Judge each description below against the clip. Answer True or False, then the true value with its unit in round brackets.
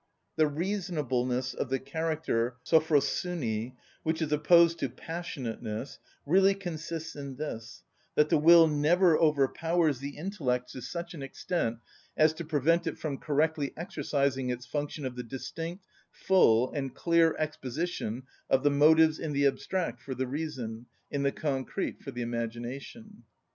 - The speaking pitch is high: False (150 Hz)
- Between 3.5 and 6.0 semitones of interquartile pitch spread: True (4.1 semitones)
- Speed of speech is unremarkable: True (145 wpm)